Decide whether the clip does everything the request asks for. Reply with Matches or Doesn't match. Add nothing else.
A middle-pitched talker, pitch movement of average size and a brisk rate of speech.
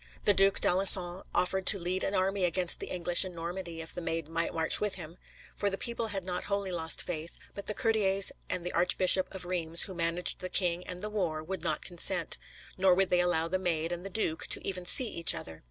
Doesn't match